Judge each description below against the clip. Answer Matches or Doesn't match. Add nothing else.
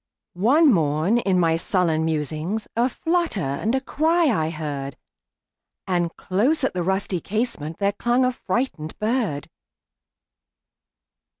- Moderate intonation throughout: Doesn't match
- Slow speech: Matches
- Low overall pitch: Doesn't match